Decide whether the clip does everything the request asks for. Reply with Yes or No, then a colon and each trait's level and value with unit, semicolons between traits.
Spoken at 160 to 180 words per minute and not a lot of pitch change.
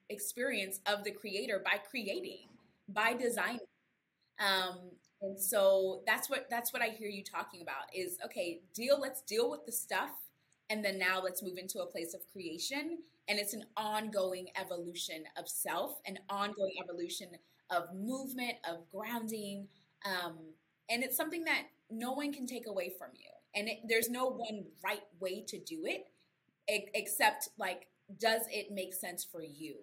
No: average, 165 wpm; average, 4.2 semitones